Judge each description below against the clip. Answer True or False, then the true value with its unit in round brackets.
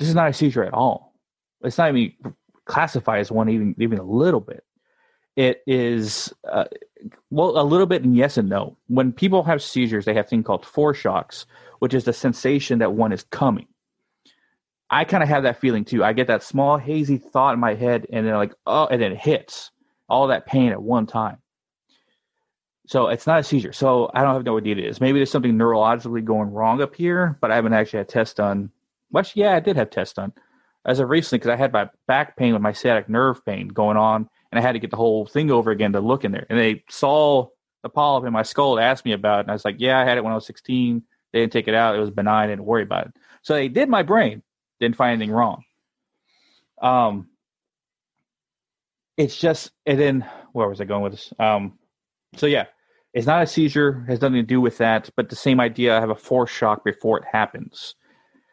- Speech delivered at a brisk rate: True (230 wpm)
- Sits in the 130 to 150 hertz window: False (120 Hz)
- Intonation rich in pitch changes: False (3.8 semitones)